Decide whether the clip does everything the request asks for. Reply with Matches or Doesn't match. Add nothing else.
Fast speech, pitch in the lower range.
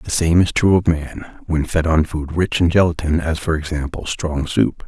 Matches